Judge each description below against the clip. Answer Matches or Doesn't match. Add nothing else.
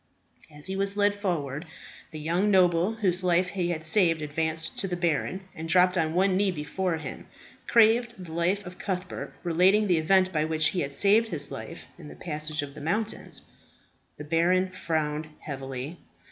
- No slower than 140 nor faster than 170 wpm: Doesn't match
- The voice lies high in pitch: Doesn't match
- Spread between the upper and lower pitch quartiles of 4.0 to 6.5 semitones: Doesn't match